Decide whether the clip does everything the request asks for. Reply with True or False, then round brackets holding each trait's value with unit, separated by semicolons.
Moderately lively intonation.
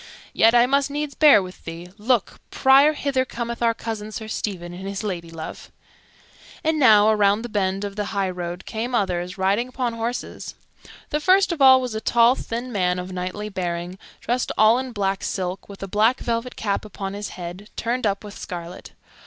True (4.4 semitones)